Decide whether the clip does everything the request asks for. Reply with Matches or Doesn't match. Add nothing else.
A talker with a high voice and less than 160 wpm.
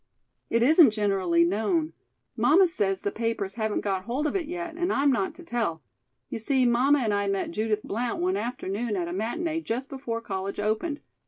Doesn't match